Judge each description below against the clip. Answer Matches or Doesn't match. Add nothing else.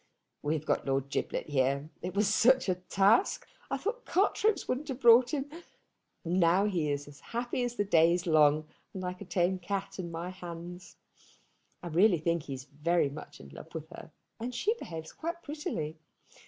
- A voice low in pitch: Doesn't match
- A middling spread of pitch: Doesn't match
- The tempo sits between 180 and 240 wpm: Matches